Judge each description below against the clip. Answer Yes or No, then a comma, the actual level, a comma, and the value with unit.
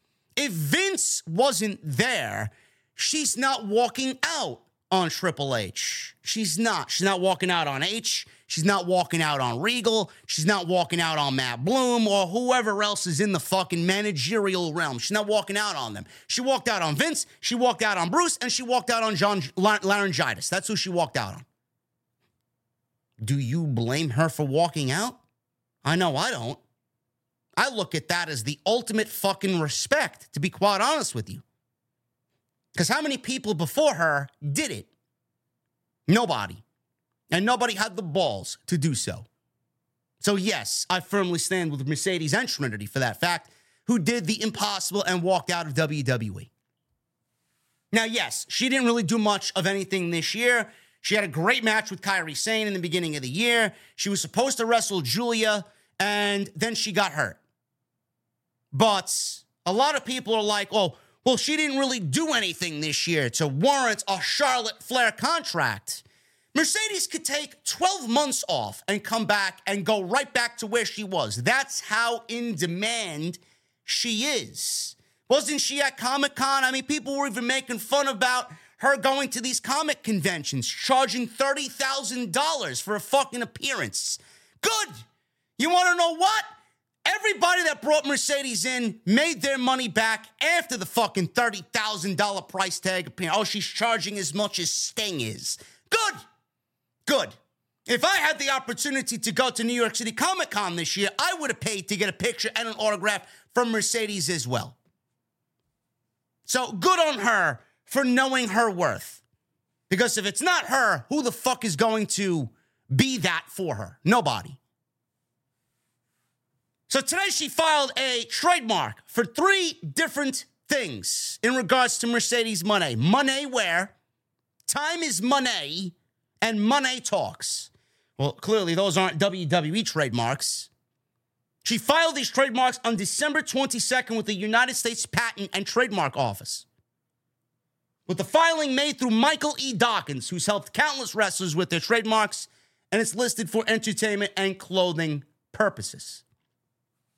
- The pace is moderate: Yes, average, 160 wpm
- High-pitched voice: Yes, high, 210 Hz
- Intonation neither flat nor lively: No, wide, 6.9 semitones